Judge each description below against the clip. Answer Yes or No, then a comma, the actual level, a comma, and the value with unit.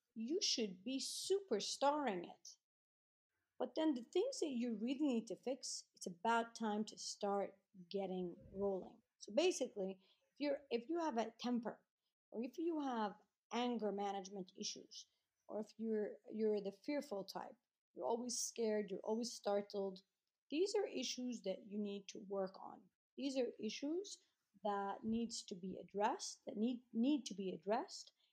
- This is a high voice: Yes, high, 225 Hz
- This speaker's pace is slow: No, average, 155 wpm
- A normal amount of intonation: Yes, average, 4.5 semitones